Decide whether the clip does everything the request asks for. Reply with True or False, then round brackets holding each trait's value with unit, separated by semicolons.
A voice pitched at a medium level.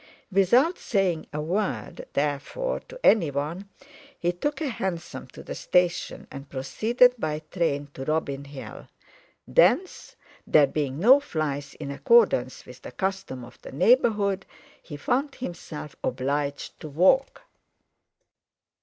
True (165 Hz)